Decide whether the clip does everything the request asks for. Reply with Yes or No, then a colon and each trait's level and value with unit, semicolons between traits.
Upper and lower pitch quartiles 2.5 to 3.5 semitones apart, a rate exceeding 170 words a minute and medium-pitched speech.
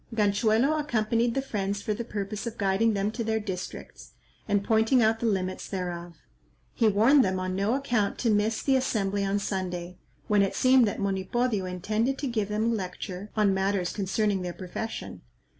No: average, 2.9 semitones; average, 180 wpm; high, 210 Hz